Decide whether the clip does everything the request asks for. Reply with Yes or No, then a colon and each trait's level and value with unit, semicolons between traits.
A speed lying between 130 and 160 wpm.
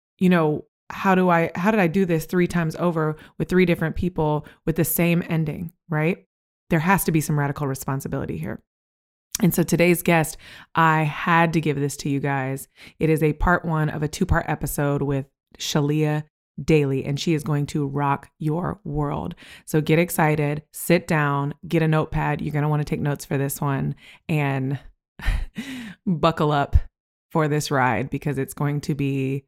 No: average, 185 wpm